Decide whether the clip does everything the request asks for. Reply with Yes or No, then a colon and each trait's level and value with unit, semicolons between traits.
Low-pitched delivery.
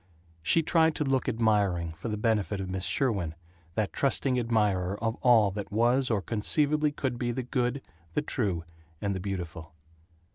Yes: low, 110 Hz